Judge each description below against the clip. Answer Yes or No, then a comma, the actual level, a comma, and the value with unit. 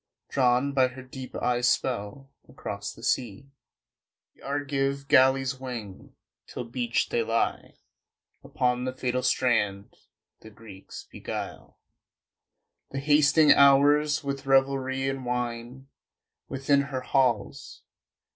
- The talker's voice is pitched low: Yes, low, 130 Hz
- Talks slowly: Yes, slow, 110 wpm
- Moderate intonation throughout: No, narrow, 2.1 semitones